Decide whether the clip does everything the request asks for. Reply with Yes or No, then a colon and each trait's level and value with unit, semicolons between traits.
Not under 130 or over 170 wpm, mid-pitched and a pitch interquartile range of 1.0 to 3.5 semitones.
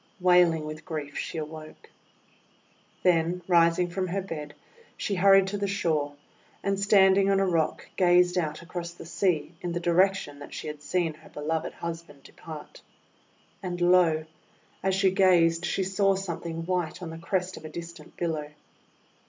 Yes: average, 160 wpm; medium, 175 Hz; narrow, 2.6 semitones